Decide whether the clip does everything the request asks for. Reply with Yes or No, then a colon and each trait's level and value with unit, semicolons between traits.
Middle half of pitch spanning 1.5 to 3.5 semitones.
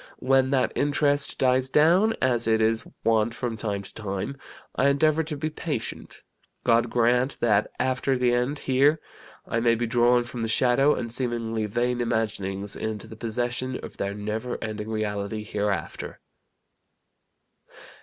Yes: average, 3.0 semitones